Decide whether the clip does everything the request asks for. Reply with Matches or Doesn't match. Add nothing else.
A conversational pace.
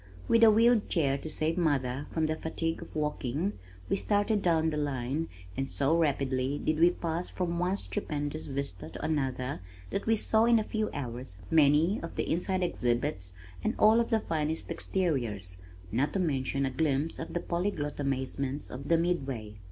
Matches